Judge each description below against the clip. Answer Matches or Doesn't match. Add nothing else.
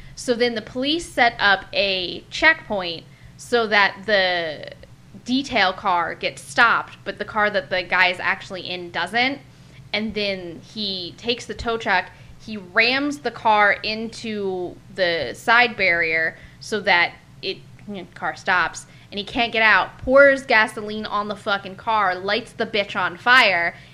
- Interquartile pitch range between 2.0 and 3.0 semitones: Doesn't match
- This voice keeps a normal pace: Matches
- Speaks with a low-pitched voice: Doesn't match